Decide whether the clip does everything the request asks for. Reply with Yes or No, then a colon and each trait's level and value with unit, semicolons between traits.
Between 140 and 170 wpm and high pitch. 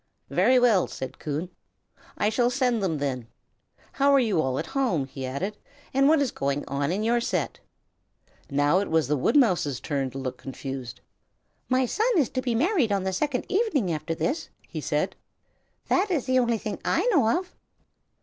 No: average, 185 wpm; high, 210 Hz